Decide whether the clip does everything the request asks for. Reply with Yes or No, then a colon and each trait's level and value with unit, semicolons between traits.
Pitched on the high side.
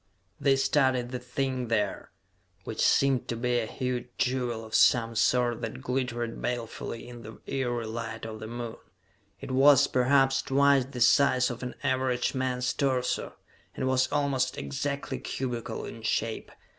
No: low, 125 Hz